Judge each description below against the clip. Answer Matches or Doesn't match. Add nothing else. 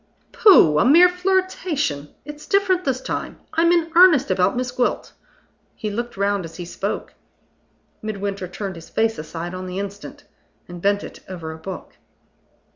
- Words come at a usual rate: Matches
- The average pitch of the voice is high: Matches